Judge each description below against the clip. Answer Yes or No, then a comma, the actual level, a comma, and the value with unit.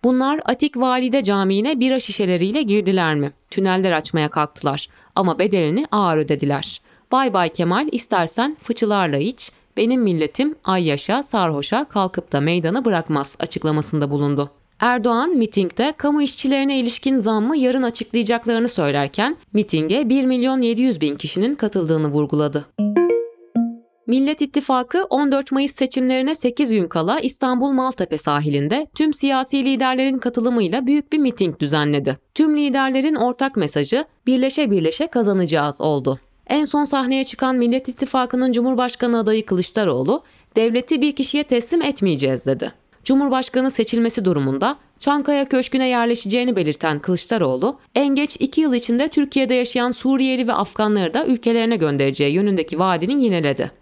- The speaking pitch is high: Yes, high, 235 Hz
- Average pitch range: No, wide, 7.2 semitones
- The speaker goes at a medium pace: Yes, average, 130 wpm